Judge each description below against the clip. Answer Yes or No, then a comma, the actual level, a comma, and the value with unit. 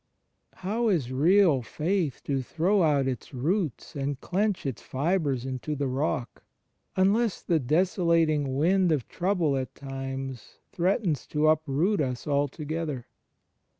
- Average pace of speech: No, slow, 130 wpm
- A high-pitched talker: No, medium, 150 Hz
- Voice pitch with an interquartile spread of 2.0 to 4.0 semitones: No, average, 5.1 semitones